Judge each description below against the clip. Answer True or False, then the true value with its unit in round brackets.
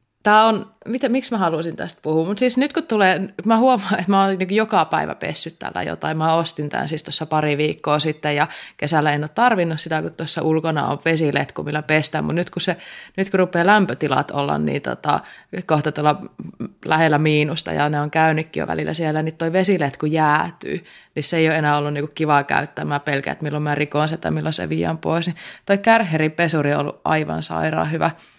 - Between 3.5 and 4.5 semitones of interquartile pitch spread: True (4.0 semitones)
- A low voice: False (160 Hz)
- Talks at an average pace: False (205 wpm)